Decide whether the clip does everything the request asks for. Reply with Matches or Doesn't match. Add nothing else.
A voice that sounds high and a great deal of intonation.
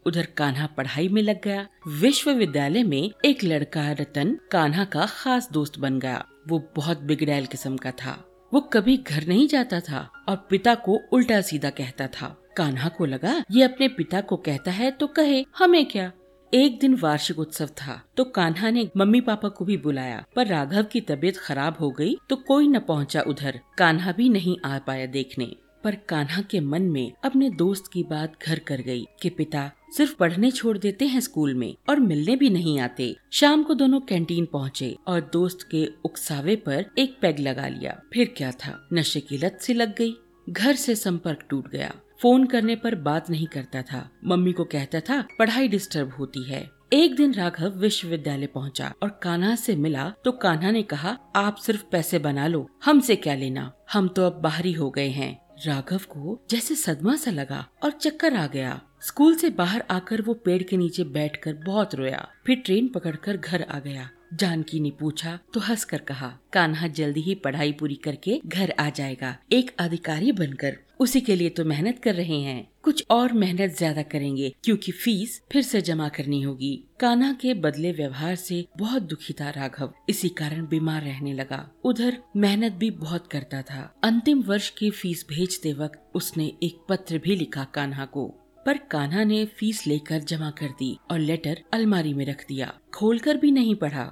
Doesn't match